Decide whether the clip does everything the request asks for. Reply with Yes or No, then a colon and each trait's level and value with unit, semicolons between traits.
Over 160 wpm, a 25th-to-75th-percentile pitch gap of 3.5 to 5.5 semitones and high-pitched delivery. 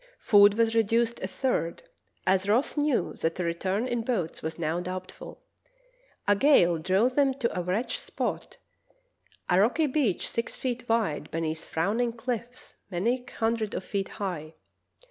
No: average, 150 wpm; average, 5.1 semitones; high, 210 Hz